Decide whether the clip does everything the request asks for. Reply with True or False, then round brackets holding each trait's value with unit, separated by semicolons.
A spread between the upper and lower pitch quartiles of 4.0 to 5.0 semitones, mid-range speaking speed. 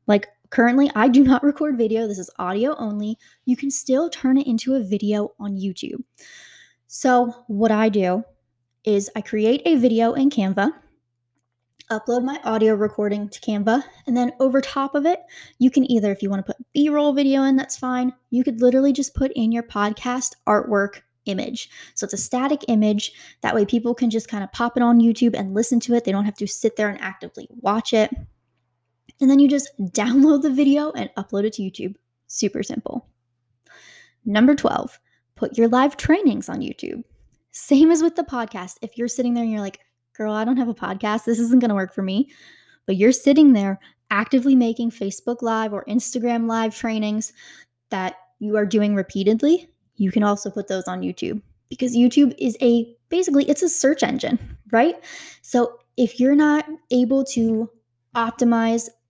True (4.4 semitones; 185 wpm)